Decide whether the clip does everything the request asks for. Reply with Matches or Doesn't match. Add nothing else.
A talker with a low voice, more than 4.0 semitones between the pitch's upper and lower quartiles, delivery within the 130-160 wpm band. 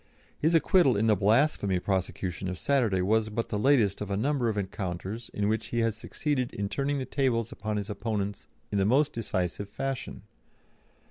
Doesn't match